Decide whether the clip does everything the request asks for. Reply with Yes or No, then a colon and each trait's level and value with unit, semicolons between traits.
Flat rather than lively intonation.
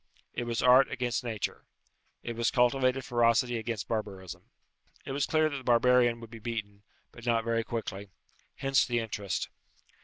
Yes: narrow, 1.9 semitones